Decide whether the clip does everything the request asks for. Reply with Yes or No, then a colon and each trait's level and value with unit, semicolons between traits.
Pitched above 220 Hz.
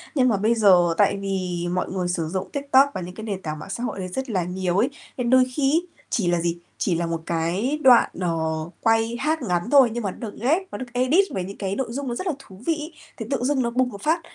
No: high, 215 Hz